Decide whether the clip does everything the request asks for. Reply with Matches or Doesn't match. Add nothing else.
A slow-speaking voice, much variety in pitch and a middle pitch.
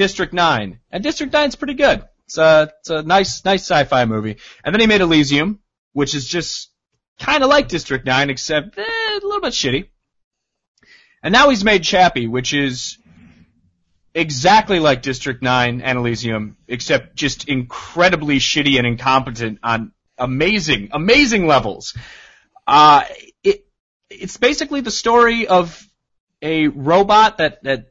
Doesn't match